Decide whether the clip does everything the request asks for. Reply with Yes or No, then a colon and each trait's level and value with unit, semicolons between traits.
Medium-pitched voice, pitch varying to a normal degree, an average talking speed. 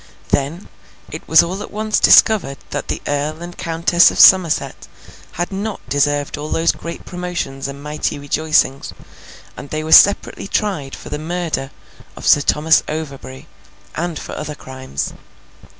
Yes: medium, 155 Hz; average, 3.5 semitones; average, 150 wpm